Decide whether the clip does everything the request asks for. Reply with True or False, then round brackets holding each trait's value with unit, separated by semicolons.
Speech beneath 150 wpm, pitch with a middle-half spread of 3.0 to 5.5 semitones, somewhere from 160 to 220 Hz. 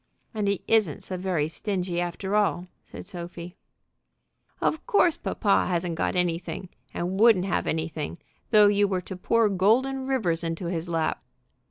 False (155 wpm; 3.3 semitones; 185 Hz)